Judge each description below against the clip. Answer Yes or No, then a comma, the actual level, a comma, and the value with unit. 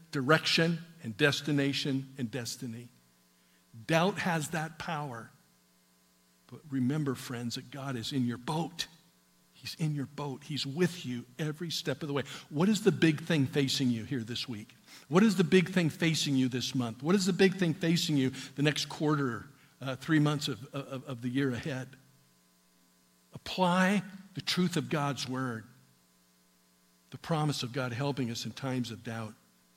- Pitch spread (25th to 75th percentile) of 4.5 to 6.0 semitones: Yes, average, 5.1 semitones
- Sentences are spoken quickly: No, average, 170 wpm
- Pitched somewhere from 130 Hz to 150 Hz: Yes, low, 135 Hz